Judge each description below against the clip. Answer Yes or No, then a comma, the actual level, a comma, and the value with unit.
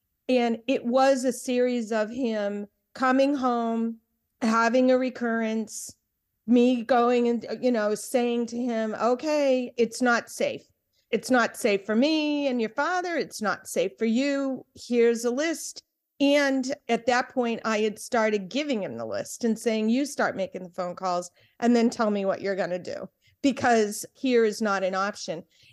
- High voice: Yes, high, 235 Hz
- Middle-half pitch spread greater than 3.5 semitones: No, average, 2.8 semitones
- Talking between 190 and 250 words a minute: No, average, 175 wpm